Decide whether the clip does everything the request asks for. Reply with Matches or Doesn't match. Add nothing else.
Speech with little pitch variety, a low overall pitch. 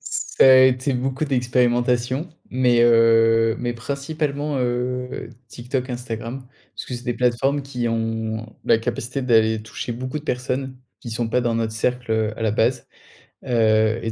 Matches